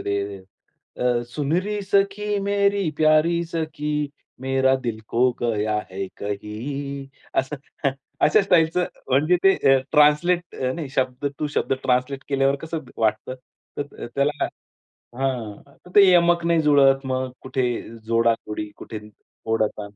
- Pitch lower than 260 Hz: Yes, medium, 140 Hz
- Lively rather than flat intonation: Yes, wide, 5.7 semitones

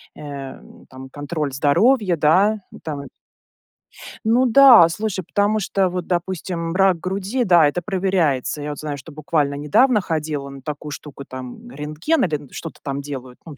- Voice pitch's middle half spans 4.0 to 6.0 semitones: Yes, average, 5.1 semitones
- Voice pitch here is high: No, medium, 160 Hz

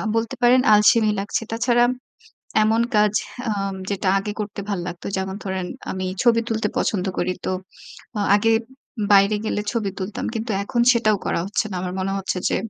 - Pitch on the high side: Yes, high, 210 Hz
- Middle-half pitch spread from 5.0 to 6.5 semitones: No, narrow, 2.6 semitones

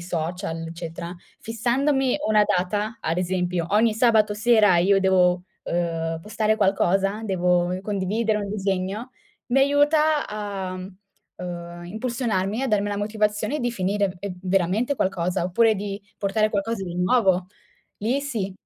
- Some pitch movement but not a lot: Yes, average, 3.3 semitones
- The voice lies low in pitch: No, high, 200 Hz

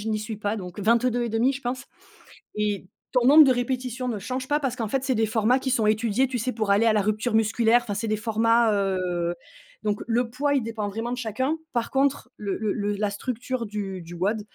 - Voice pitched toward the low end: No, high, 225 Hz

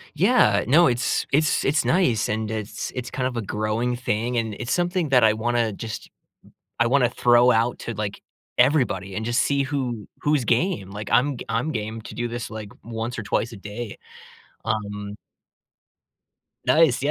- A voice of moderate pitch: No, low, 120 Hz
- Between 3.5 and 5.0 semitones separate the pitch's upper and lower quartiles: No, average, 3.1 semitones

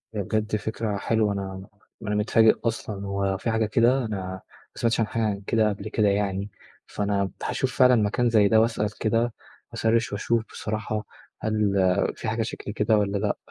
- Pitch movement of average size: No, narrow, 1.9 semitones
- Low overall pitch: Yes, low, 105 Hz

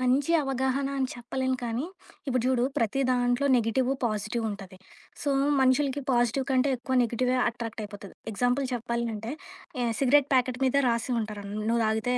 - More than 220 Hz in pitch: Yes, high, 245 Hz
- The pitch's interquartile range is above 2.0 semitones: Yes, narrow, 2.4 semitones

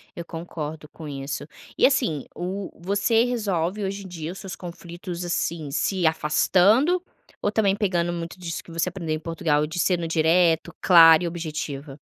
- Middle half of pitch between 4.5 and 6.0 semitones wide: No, average, 3.1 semitones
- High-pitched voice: No, medium, 170 Hz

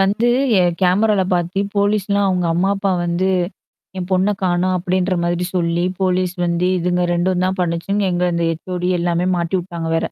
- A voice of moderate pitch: Yes, medium, 180 Hz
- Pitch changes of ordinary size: No, narrow, 1.6 semitones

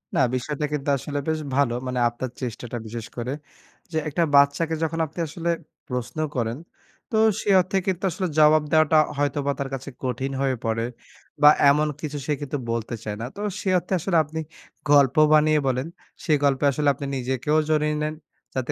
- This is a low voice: No, medium, 145 Hz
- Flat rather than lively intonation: No, average, 3.4 semitones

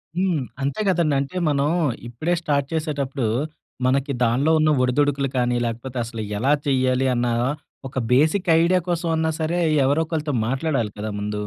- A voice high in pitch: No, medium, 140 Hz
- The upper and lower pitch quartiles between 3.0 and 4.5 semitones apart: Yes, average, 3.9 semitones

